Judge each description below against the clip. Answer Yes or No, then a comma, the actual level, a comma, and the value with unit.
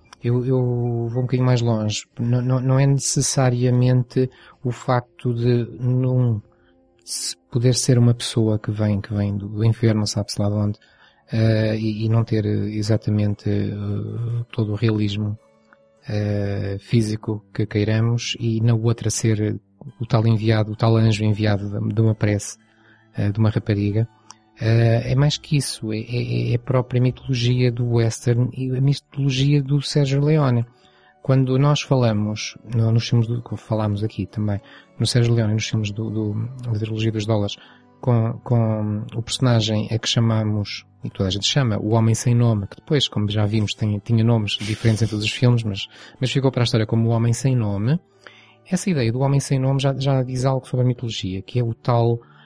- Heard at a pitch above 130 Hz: No, low, 115 Hz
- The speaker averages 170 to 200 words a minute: Yes, average, 180 wpm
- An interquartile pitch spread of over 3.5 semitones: No, average, 2.7 semitones